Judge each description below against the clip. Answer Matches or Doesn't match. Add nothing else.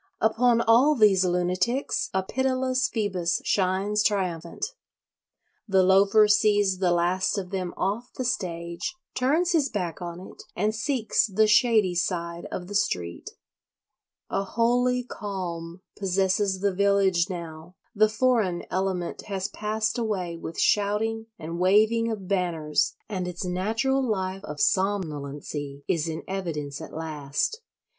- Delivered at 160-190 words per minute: Doesn't match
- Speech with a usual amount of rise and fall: Matches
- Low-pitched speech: Doesn't match